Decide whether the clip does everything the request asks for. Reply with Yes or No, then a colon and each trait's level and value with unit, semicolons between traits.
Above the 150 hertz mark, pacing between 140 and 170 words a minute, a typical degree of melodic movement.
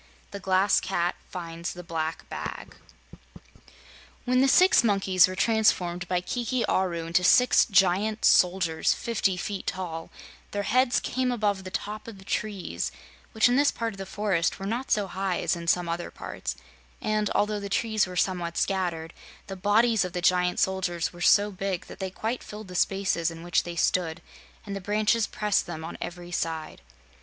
No: high, 190 Hz; average, 180 wpm; average, 3.3 semitones